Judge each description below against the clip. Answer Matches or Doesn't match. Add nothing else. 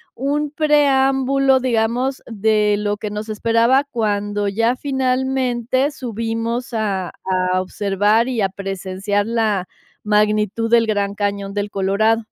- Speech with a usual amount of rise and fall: Matches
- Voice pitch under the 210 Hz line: Doesn't match